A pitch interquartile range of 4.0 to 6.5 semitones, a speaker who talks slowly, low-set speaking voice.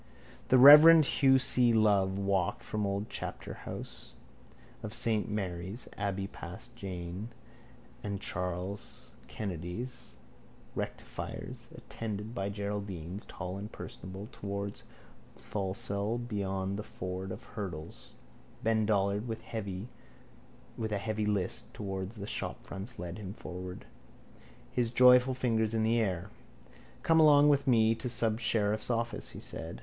No: average, 3.0 semitones; slow, 125 wpm; low, 105 Hz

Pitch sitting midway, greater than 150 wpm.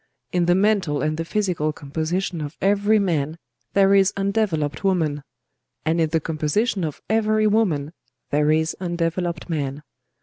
No: medium, 170 Hz; average, 145 wpm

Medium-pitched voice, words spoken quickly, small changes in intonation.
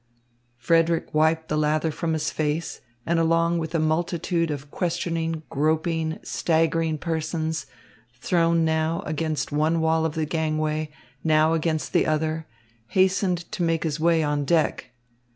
No: medium, 160 Hz; average, 140 wpm; narrow, 1.1 semitones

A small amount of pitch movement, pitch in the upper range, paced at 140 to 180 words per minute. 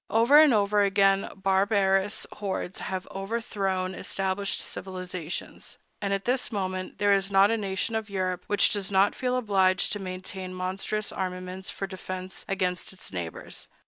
Yes: narrow, 1.6 semitones; high, 195 Hz; average, 150 wpm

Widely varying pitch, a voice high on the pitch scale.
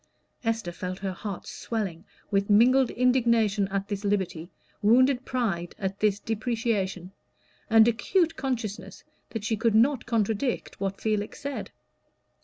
No: average, 3.3 semitones; high, 220 Hz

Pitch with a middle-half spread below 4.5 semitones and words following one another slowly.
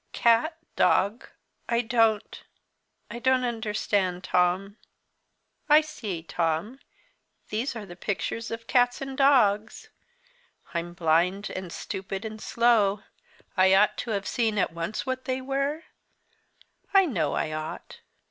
No: average, 4.8 semitones; slow, 130 wpm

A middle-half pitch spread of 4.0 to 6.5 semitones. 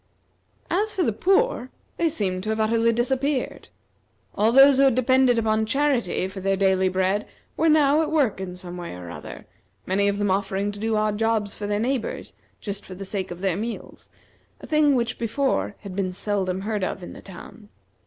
Yes: average, 5.1 semitones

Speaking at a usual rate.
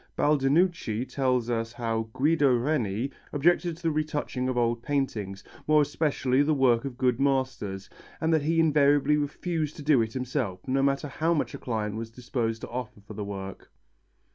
Yes: average, 175 wpm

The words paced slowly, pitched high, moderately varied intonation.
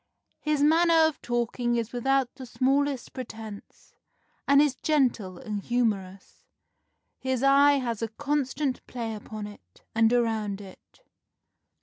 Yes: slow, 125 wpm; high, 245 Hz; average, 4.0 semitones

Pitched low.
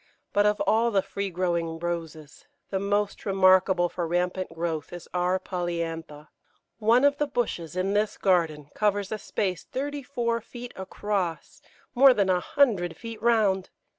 No: high, 190 Hz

